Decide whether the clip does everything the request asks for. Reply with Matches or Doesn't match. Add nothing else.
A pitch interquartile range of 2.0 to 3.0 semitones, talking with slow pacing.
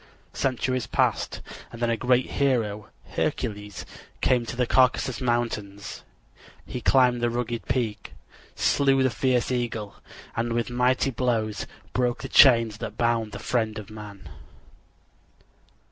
Matches